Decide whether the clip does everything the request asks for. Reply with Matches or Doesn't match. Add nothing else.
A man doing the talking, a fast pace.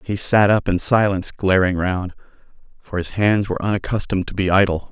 Doesn't match